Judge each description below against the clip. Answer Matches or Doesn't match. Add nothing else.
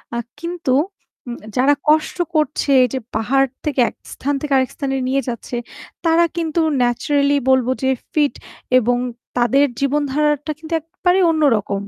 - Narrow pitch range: Doesn't match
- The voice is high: Matches